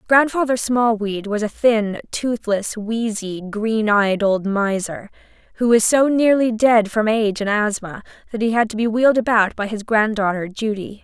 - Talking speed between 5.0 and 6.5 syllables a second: No, 4.6 syllables/s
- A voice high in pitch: Yes, high, 220 Hz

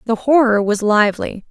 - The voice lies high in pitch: Yes, high, 225 Hz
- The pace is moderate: Yes, average, 160 wpm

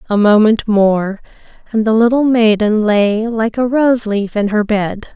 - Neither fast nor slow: Yes, average, 175 wpm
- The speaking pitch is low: No, high, 215 Hz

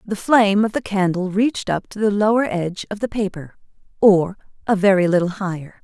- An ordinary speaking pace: Yes, average, 195 wpm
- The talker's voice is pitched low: No, high, 200 Hz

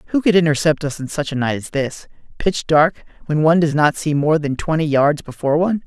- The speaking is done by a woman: No, male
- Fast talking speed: Yes, fast, 235 wpm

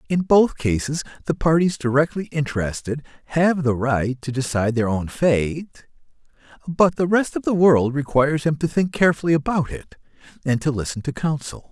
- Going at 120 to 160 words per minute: No, average, 170 wpm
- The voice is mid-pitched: Yes, medium, 145 Hz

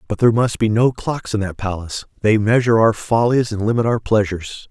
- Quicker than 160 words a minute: Yes, fast, 205 wpm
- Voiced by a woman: No, male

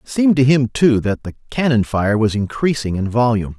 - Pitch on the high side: No, low, 120 Hz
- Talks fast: Yes, fast, 220 wpm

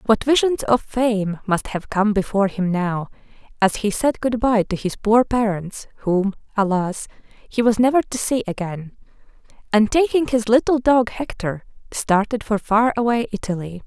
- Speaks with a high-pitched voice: Yes, high, 215 Hz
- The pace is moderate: Yes, average, 165 wpm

